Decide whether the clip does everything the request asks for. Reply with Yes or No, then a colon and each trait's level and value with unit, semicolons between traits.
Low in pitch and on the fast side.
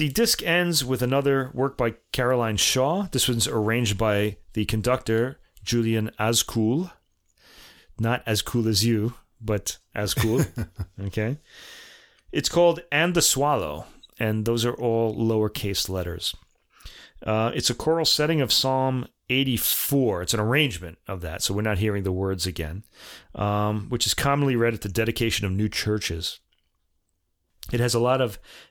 No: low, 115 Hz; average, 155 wpm